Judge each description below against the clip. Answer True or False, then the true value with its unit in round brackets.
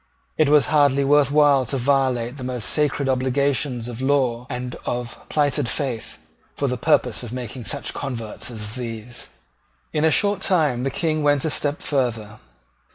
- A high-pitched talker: False (135 Hz)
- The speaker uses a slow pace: False (165 wpm)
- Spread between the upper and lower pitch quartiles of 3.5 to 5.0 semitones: False (3.0 semitones)